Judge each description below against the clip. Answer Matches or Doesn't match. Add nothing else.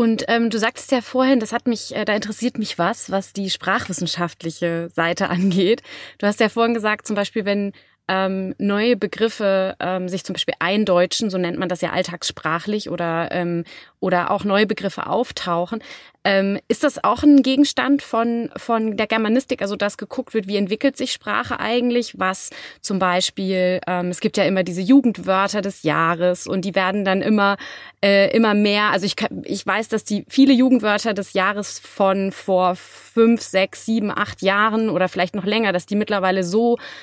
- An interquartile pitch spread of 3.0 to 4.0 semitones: Matches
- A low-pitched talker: Doesn't match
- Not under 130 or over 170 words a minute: Doesn't match